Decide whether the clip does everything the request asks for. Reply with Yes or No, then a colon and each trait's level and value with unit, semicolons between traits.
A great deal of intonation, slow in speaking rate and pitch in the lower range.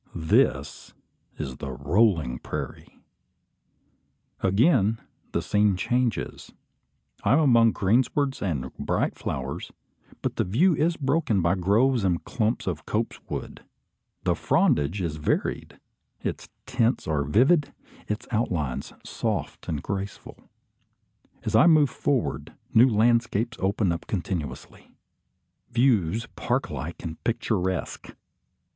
Yes: wide, 6.2 semitones; slow, 115 wpm; low, 105 Hz